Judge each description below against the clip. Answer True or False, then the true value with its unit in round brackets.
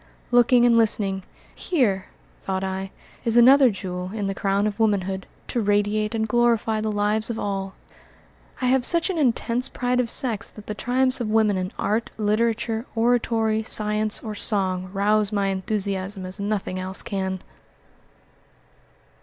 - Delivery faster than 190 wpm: False (155 wpm)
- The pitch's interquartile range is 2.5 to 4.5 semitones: True (3.1 semitones)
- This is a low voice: False (215 Hz)